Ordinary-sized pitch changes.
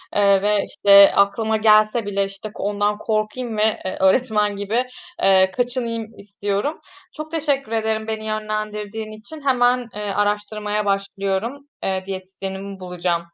No: narrow, 2.0 semitones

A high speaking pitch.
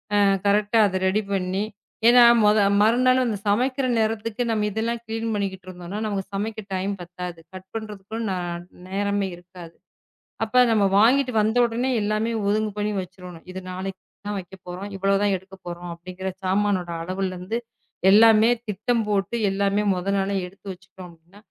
Yes: high, 200 Hz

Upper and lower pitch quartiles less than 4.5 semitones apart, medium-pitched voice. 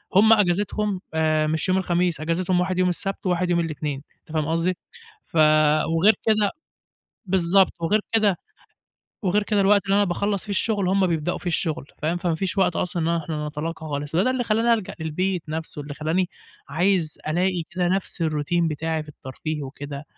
Yes: average, 3.5 semitones; medium, 175 Hz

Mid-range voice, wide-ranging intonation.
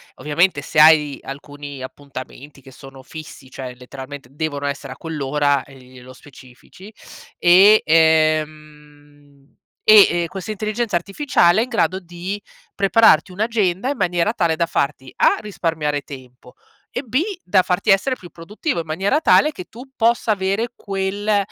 Yes: medium, 160 Hz; wide, 5.8 semitones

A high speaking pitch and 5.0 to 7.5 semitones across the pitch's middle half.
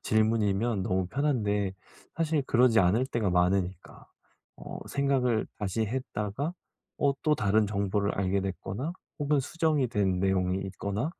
No: low, 105 Hz; average, 5.3 semitones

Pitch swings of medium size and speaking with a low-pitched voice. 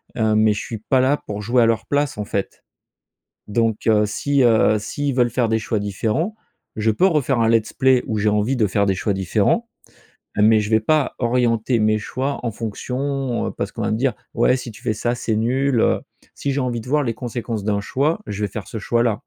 Yes: average, 3.3 semitones; low, 115 Hz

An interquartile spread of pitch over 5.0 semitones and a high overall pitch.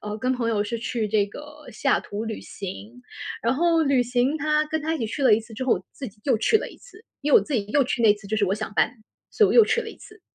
Yes: wide, 5.6 semitones; high, 245 Hz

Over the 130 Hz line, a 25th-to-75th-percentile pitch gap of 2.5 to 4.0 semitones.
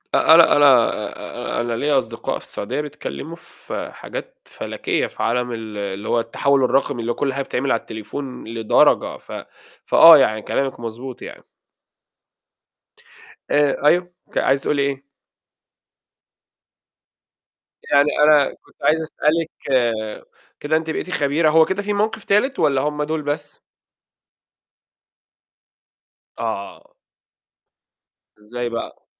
No: medium, 140 Hz; average, 4.9 semitones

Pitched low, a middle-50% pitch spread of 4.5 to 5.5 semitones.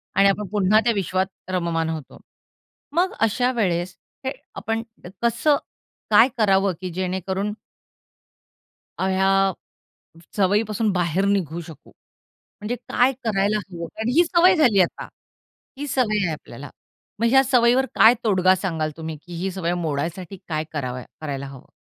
No: high, 195 Hz; average, 4.8 semitones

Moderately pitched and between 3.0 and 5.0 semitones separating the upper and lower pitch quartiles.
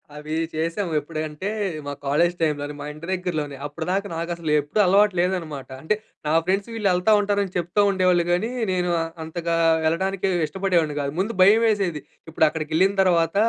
Yes: medium, 175 Hz; average, 3.5 semitones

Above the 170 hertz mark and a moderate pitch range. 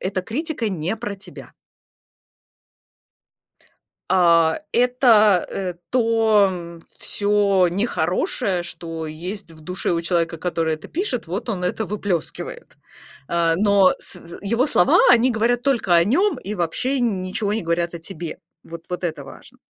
Yes: high, 190 Hz; average, 4.7 semitones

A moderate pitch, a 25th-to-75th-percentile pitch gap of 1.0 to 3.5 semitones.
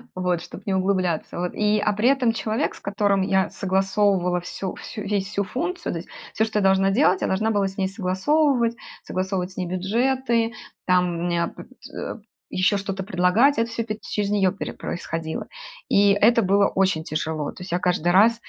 No: high, 195 Hz; average, 2.9 semitones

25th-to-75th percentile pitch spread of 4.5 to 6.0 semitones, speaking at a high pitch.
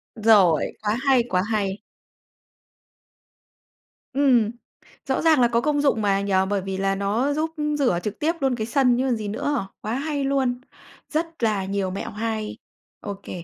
Yes: average, 5.2 semitones; high, 225 Hz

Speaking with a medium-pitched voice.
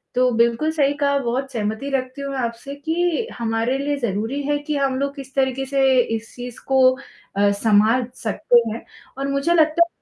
No: very high, 270 Hz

